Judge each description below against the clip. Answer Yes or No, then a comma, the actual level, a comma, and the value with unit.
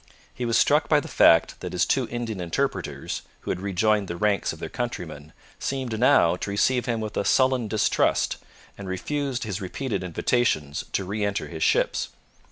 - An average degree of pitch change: Yes, average, 4.9 semitones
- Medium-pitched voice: No, low, 105 Hz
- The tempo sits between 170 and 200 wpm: Yes, average, 180 wpm